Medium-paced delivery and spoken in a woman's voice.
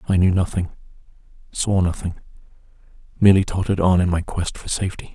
No: average, 150 wpm; male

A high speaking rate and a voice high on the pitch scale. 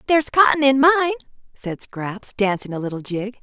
No: average, 175 wpm; high, 245 Hz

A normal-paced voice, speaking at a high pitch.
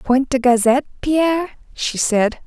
Yes: average, 145 wpm; very high, 265 Hz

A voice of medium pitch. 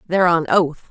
Yes: medium, 165 Hz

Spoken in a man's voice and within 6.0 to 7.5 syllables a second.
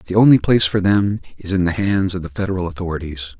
Yes: male; 6.9 syllables/s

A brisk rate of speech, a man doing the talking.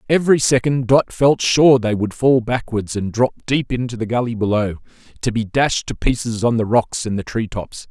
Yes: fast, 215 wpm; male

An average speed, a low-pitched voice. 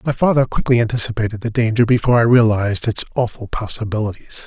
Yes: average, 160 wpm; low, 115 Hz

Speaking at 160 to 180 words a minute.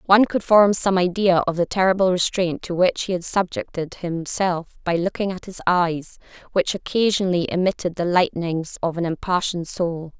Yes: average, 170 wpm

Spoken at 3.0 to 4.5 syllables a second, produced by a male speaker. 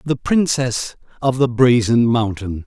Yes: 3.9 syllables/s; male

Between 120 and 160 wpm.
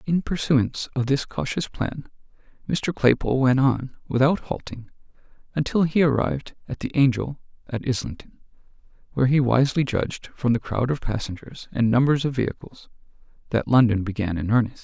Yes: average, 155 wpm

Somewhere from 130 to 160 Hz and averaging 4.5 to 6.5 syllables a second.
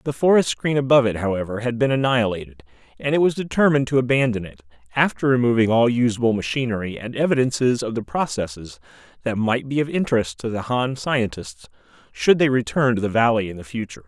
No: low, 120 Hz; 6.3 syllables/s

